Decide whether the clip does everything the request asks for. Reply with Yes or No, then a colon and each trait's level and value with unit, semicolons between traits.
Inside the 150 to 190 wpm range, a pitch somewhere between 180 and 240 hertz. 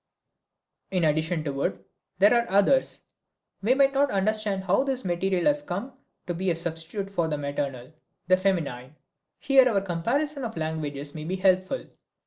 Yes: average, 160 wpm; medium, 185 Hz